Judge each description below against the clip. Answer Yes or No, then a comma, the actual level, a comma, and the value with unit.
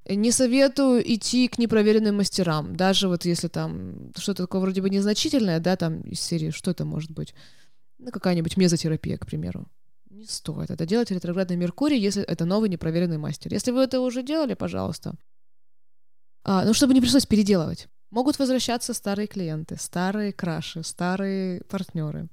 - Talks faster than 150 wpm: Yes, fast, 160 wpm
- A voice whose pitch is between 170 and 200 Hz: Yes, high, 190 Hz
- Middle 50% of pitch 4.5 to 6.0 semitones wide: Yes, average, 5.0 semitones